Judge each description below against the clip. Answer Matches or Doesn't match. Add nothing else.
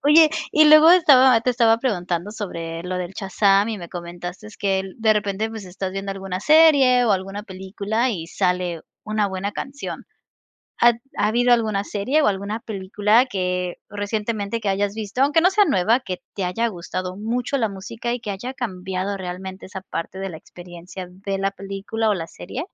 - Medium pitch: Doesn't match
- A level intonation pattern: Doesn't match